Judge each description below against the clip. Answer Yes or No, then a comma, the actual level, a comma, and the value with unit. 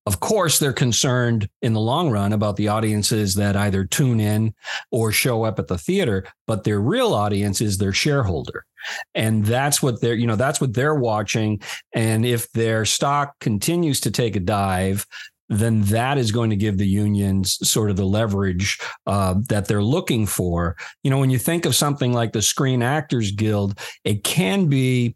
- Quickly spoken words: No, average, 190 wpm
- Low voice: Yes, low, 110 Hz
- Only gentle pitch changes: No, average, 3.9 semitones